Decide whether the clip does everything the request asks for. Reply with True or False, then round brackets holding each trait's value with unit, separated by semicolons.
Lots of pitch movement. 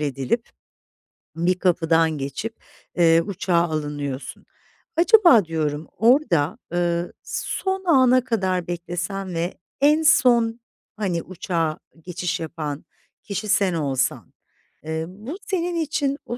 True (6.3 semitones)